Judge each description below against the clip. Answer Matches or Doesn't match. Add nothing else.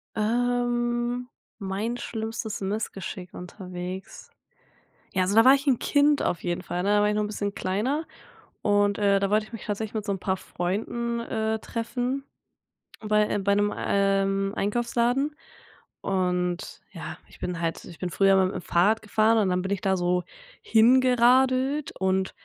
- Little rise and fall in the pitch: Doesn't match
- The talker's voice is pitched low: Doesn't match